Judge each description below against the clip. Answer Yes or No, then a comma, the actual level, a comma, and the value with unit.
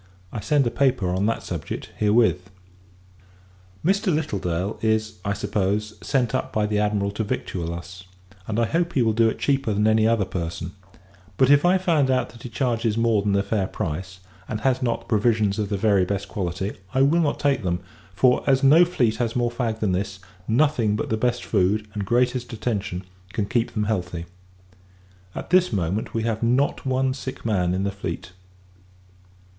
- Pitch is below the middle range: Yes, low, 110 Hz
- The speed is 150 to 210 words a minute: Yes, average, 190 wpm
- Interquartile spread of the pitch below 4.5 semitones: Yes, average, 4.1 semitones